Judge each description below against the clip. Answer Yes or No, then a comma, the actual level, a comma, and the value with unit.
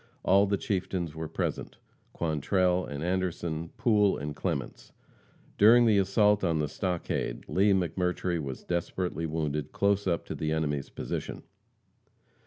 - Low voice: Yes, very low, 90 Hz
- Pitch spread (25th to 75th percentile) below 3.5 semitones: No, average, 3.8 semitones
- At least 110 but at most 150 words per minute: Yes, slow, 135 wpm